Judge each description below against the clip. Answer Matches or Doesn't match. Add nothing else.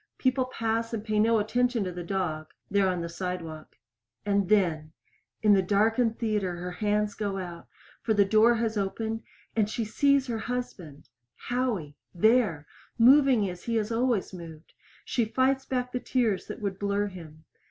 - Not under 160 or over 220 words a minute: Matches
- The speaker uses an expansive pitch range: Doesn't match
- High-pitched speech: Matches